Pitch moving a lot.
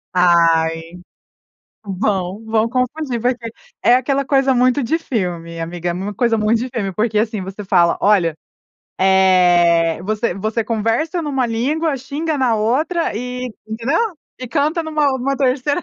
Yes: wide, 5.9 semitones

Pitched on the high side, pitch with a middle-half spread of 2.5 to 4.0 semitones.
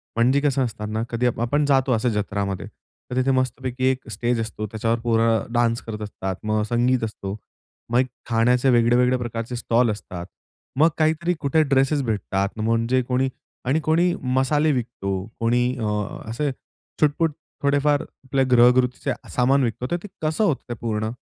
No: low, 125 Hz; average, 3.0 semitones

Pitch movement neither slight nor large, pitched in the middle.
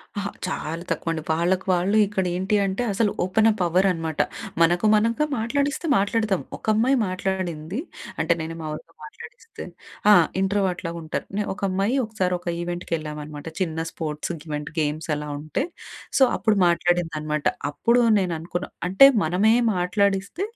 Yes: average, 3.9 semitones; medium, 180 Hz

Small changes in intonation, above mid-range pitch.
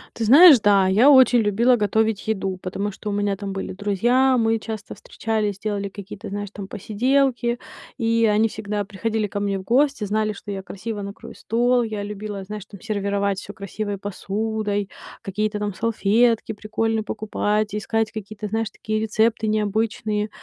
Yes: narrow, 1.8 semitones; high, 210 Hz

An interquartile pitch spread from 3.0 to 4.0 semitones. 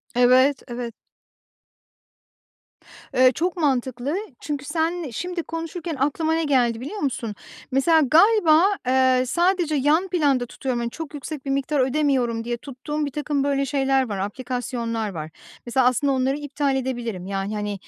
Yes: average, 3.7 semitones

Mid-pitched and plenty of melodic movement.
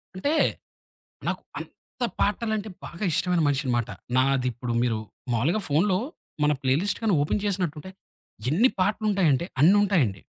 Yes: medium, 170 Hz; wide, 7.1 semitones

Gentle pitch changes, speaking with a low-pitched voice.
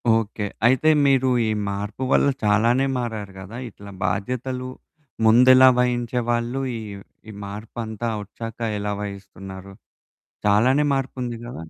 No: average, 3.7 semitones; low, 115 Hz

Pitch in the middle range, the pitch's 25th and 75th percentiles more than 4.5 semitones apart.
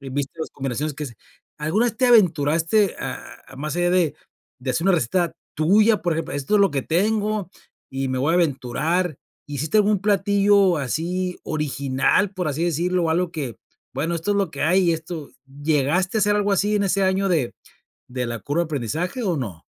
Yes: medium, 165 Hz; average, 5.2 semitones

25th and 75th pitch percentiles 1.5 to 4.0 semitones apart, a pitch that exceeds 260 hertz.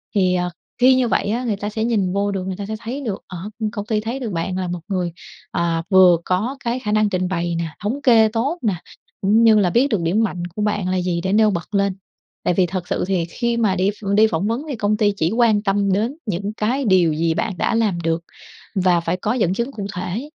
No: average, 3.7 semitones; high, 205 Hz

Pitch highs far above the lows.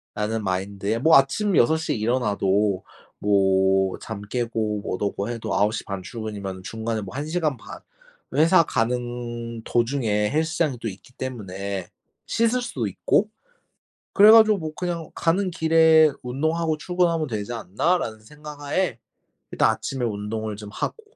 Yes: wide, 7.3 semitones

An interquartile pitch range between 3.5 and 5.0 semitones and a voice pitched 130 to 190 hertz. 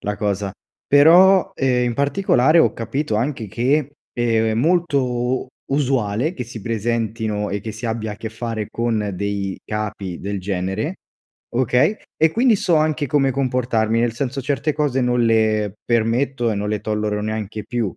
No: average, 4.2 semitones; low, 115 Hz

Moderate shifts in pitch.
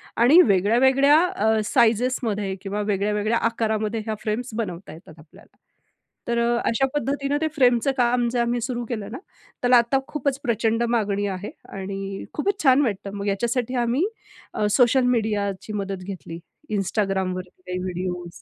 Yes: average, 3.7 semitones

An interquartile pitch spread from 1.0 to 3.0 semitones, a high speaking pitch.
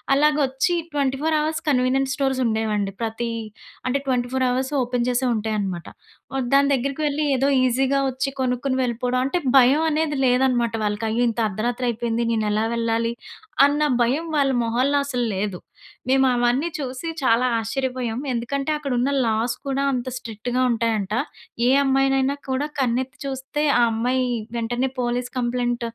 Yes: narrow, 2.6 semitones; very high, 250 Hz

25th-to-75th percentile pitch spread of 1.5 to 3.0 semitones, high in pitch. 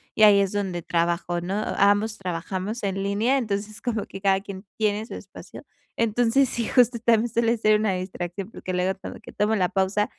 Yes: average, 2.7 semitones; high, 205 Hz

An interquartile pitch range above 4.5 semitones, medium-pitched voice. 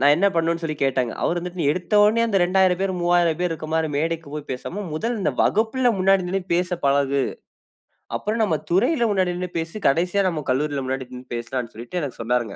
Yes: average, 5.2 semitones; medium, 170 Hz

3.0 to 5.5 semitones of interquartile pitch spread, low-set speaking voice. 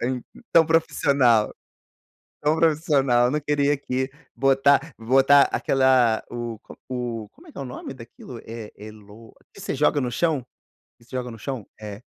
Yes: average, 3.4 semitones; low, 130 Hz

